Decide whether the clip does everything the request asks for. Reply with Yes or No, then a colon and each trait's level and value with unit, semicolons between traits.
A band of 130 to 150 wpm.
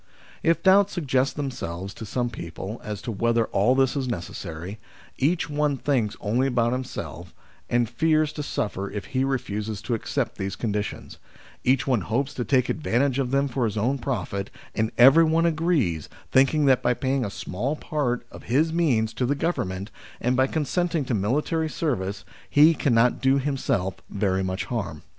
No: average, 175 wpm